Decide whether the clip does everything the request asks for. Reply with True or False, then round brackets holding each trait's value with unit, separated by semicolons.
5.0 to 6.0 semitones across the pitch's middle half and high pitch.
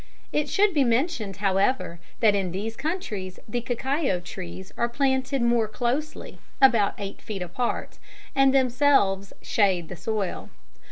True (5.5 semitones; 230 Hz)